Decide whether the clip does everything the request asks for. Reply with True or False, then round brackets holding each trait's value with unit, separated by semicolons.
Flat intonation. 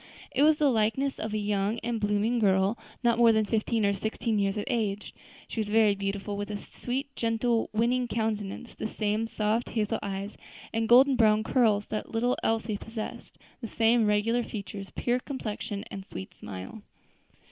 True (2.3 semitones)